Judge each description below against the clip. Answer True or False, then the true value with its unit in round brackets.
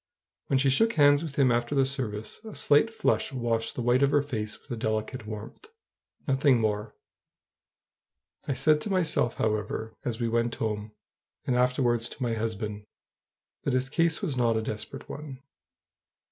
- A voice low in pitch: True (125 Hz)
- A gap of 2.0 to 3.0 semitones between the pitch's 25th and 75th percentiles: False (4.1 semitones)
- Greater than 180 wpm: False (170 wpm)